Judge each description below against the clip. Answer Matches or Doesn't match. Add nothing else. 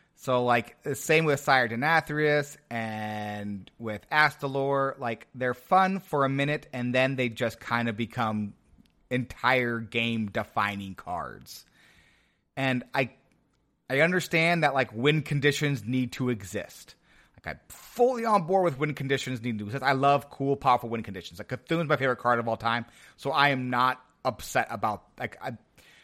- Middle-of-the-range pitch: Doesn't match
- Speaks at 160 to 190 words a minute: Matches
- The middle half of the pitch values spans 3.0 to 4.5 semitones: Matches